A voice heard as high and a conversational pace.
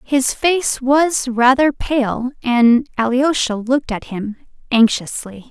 No: very high, 255 Hz; slow, 120 wpm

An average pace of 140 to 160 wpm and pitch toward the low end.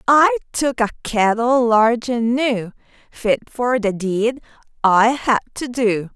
No: average, 145 wpm; high, 235 Hz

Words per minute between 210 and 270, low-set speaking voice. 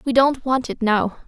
No: fast, 235 wpm; high, 245 Hz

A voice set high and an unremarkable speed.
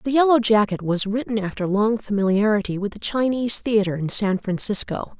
Yes: high, 215 Hz; average, 175 wpm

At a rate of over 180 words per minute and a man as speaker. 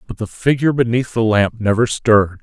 Yes: average, 200 wpm; male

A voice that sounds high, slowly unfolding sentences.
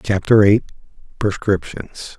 No: low, 100 Hz; slow, 80 wpm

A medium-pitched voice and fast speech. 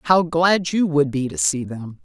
Yes: medium, 145 Hz; fast, 235 wpm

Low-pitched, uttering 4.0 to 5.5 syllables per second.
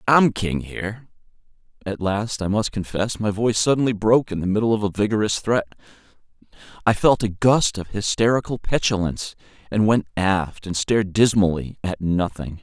Yes: low, 105 Hz; 5.3 syllables/s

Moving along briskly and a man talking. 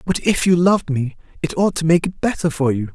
Yes: fast, 265 wpm; male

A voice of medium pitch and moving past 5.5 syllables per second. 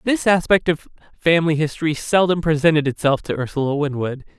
Yes: medium, 155 Hz; 6.0 syllables/s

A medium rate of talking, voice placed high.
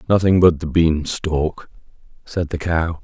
No: average, 160 wpm; very low, 80 Hz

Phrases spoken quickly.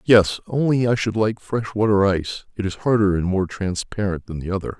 Yes: fast, 215 wpm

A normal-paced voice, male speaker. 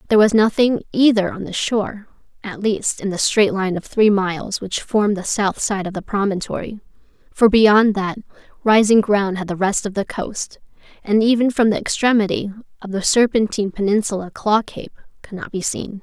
No: average, 185 wpm; female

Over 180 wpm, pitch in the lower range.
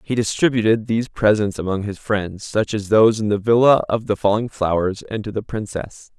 Yes: fast, 205 wpm; low, 105 Hz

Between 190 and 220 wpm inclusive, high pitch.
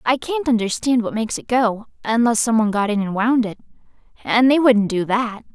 Yes: fast, 205 wpm; high, 230 Hz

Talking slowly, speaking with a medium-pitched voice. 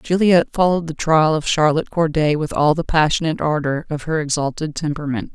No: average, 180 wpm; medium, 155 Hz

